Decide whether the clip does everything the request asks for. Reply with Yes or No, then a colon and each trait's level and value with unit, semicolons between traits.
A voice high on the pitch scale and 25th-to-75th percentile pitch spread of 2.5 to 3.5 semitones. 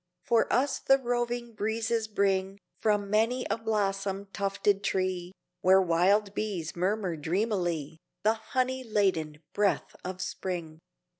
Yes: high, 200 Hz; average, 3.2 semitones